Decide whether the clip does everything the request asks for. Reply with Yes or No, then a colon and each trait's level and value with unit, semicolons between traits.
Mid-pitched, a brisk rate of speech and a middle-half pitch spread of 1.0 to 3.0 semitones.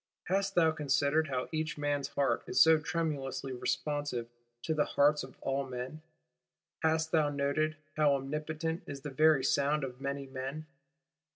No: medium, 145 Hz; average, 155 wpm; narrow, 2.4 semitones